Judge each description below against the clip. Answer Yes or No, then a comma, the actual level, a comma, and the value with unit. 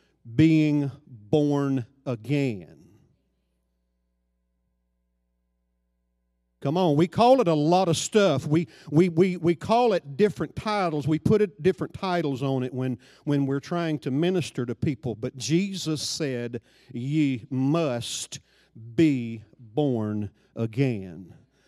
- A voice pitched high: No, medium, 140 Hz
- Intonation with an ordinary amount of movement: No, wide, 5.9 semitones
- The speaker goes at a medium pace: No, slow, 120 wpm